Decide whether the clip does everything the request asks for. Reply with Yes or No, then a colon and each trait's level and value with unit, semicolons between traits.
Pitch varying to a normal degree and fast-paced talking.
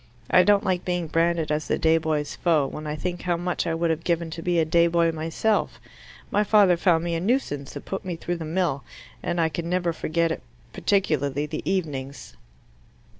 No: narrow, 2.1 semitones; fast, 210 wpm